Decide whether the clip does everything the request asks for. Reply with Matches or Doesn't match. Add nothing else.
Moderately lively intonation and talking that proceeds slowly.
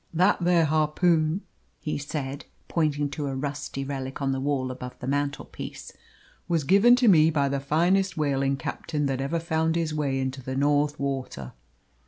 Doesn't match